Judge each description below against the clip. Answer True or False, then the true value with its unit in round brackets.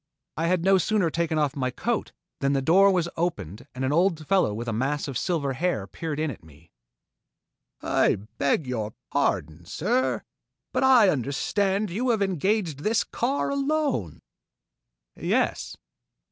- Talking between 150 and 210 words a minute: True (155 wpm)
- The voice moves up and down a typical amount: False (7.0 semitones)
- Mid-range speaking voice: True (165 Hz)